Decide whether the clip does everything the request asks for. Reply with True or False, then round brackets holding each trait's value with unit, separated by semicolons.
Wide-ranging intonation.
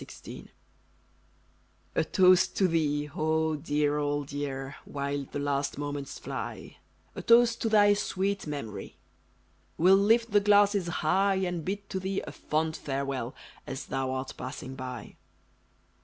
True (5.7 semitones)